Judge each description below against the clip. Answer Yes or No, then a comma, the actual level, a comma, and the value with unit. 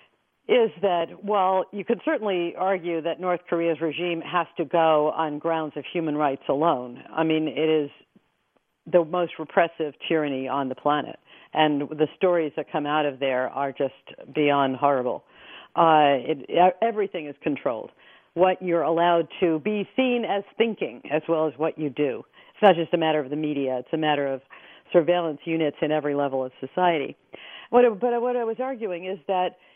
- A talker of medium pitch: Yes, medium, 165 Hz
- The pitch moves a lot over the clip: No, average, 3.5 semitones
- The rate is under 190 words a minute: Yes, average, 180 wpm